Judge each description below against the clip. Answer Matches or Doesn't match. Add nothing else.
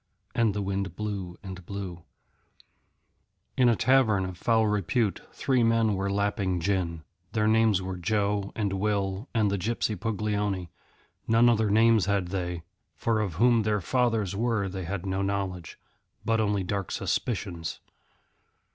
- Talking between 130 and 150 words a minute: Matches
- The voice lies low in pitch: Matches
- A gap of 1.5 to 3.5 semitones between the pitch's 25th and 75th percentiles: Matches